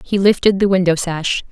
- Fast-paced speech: No, average, 195 wpm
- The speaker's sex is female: Yes, female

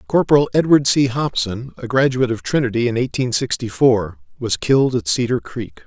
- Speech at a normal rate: Yes, average, 175 wpm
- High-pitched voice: No, low, 120 Hz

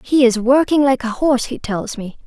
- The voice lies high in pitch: Yes, very high, 250 Hz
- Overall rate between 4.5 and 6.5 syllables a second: Yes, 5.2 syllables/s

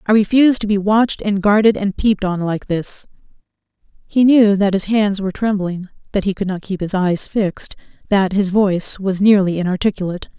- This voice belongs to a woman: Yes, female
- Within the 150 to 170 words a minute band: No, average, 190 wpm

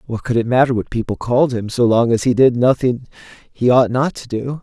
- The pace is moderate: No, fast, 245 wpm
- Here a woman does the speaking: No, male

